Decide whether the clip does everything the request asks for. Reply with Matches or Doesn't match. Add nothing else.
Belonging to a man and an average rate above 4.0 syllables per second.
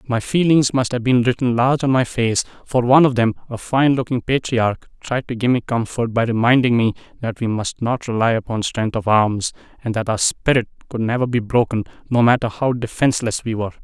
Matches